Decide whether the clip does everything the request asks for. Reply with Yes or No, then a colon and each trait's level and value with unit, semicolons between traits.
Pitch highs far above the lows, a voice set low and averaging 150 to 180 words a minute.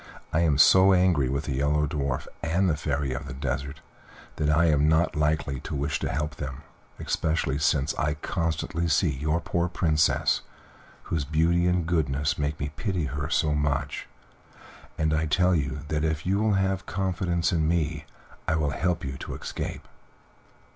No: average, 2.8 semitones; very low, 75 Hz; average, 175 wpm